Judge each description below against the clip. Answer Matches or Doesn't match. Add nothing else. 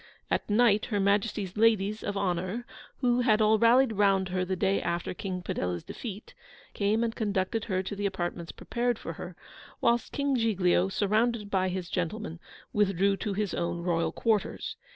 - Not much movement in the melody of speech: Doesn't match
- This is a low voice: Doesn't match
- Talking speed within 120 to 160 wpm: Doesn't match